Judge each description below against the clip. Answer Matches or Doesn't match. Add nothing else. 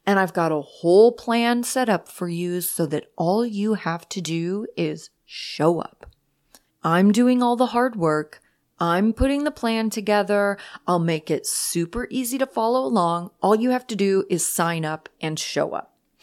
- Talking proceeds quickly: Doesn't match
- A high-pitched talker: Matches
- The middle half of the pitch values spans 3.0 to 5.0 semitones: Doesn't match